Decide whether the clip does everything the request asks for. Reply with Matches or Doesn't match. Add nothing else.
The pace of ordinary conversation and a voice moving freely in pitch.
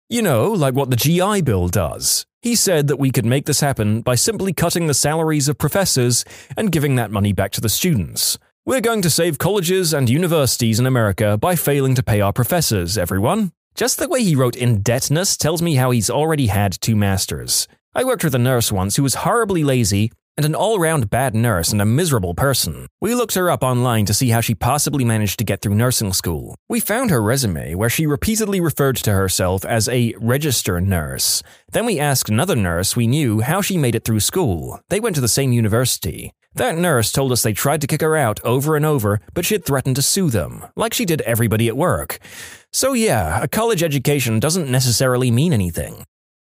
Doesn't match